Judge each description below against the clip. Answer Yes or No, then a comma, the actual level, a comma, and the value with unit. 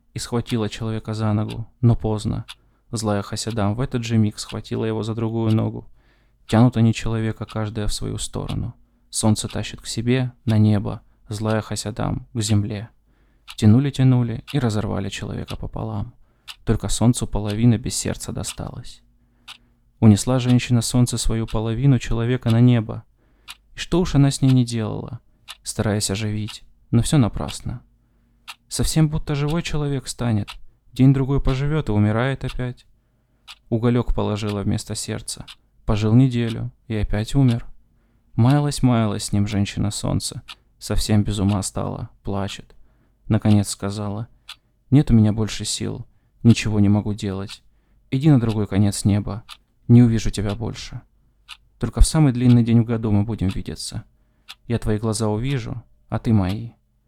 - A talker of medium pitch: No, low, 115 Hz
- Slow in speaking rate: No, average, 140 wpm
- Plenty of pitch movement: No, narrow, 2.4 semitones